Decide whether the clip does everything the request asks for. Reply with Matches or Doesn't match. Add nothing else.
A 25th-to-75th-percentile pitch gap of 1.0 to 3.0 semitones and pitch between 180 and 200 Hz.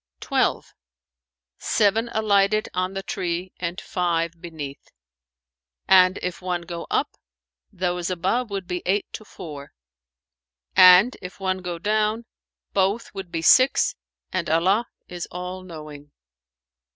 Matches